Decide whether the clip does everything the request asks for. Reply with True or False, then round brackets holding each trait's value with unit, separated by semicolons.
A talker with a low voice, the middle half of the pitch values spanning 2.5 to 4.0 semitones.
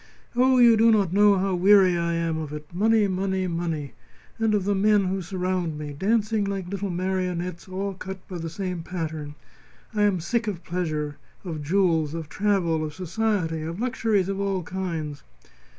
False (185 Hz; 3.3 semitones)